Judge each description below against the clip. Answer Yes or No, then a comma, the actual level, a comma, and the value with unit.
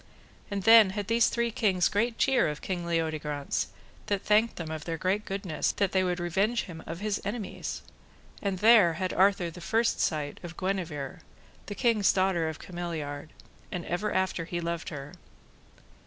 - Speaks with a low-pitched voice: No, medium, 185 Hz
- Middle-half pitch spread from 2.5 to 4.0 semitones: Yes, average, 3.7 semitones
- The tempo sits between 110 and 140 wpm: No, average, 170 wpm